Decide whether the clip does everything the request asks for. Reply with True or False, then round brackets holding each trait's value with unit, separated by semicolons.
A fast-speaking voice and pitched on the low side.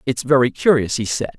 True (215 wpm; 130 Hz)